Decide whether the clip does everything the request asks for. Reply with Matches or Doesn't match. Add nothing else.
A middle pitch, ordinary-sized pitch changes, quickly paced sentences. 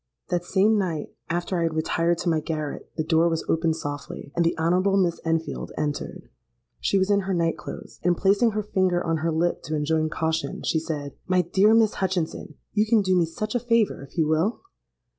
Matches